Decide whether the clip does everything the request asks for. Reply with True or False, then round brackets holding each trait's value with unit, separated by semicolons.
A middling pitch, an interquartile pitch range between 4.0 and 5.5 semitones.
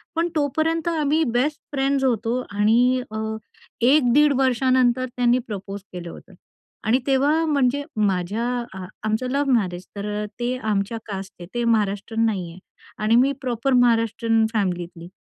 False (240 Hz; 4.3 semitones)